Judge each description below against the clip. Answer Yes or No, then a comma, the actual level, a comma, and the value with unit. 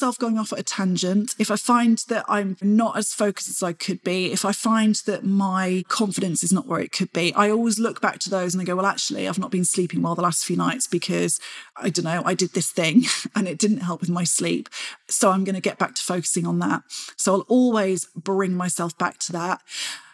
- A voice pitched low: No, high, 190 Hz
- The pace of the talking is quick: Yes, fast, 245 wpm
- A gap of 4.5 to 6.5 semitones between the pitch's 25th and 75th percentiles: No, average, 2.8 semitones